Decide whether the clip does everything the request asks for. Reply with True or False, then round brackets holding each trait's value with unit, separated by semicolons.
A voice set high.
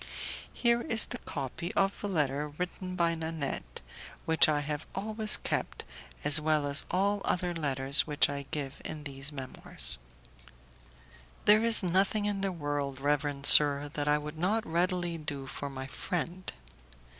False (155 Hz)